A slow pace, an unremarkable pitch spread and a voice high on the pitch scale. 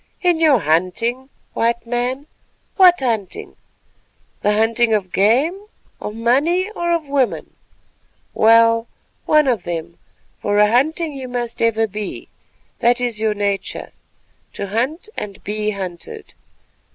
Yes: slow, 130 wpm; average, 4.9 semitones; high, 230 Hz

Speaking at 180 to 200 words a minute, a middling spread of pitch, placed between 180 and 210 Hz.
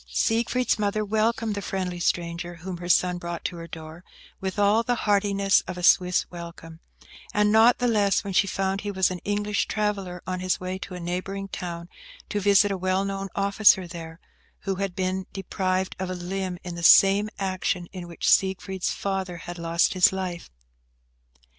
No: average, 185 wpm; narrow, 2.2 semitones; high, 190 Hz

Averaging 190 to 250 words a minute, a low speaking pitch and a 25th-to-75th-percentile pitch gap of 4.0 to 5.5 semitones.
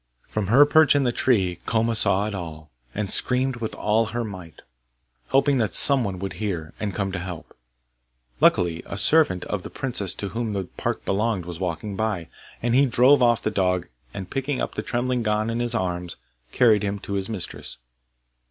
Yes: average, 195 wpm; low, 105 Hz; average, 4.3 semitones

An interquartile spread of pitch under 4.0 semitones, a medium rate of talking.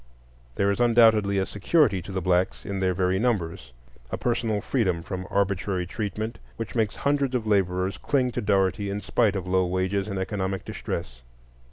Yes: average, 2.9 semitones; average, 170 wpm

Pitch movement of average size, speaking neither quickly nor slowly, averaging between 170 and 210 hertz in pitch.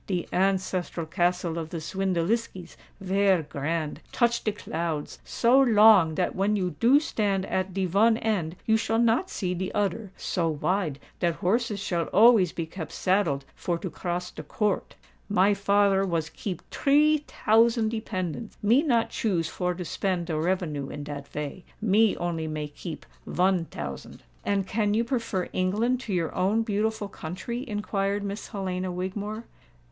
Yes: average, 4.0 semitones; average, 150 wpm; high, 190 Hz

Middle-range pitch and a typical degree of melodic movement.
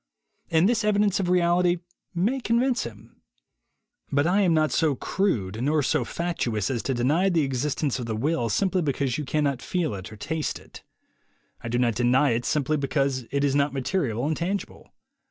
No: medium, 150 Hz; wide, 5.8 semitones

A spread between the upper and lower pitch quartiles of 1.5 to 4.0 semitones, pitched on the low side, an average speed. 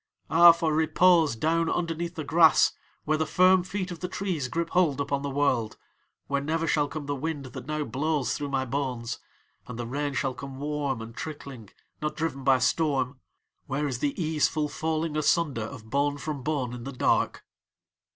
No: average, 3.2 semitones; medium, 145 Hz; average, 185 wpm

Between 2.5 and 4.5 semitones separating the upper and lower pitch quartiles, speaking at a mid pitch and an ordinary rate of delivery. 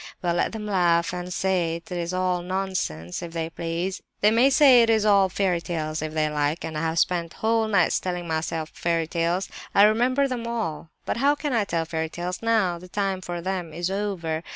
No: average, 3.7 semitones; medium, 180 Hz; fast, 215 wpm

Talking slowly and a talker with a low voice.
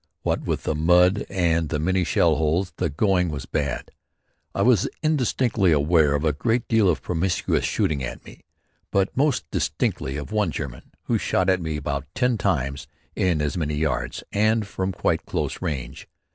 No: average, 175 wpm; very low, 85 Hz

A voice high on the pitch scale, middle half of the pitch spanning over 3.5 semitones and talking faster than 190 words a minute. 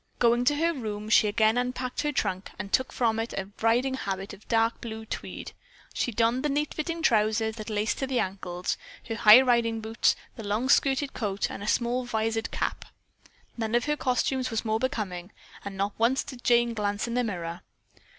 No: high, 225 Hz; average, 3.0 semitones; average, 200 wpm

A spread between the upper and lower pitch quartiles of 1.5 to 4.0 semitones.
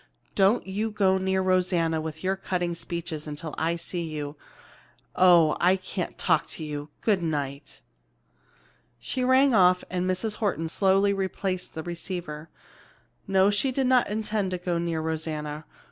Yes: average, 3.3 semitones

